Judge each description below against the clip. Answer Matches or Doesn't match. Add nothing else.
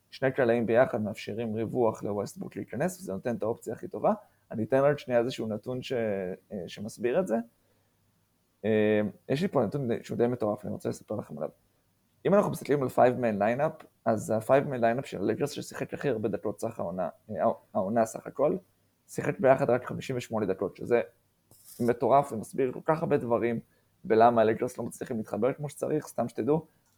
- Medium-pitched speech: Doesn't match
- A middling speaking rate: Matches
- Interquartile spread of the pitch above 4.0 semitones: Doesn't match